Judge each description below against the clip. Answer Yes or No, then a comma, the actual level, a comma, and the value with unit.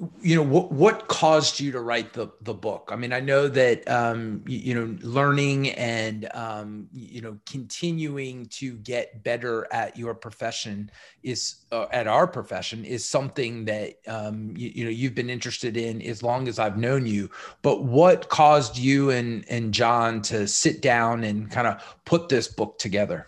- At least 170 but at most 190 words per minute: Yes, average, 185 wpm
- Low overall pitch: Yes, low, 120 Hz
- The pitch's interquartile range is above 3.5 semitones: No, average, 3.2 semitones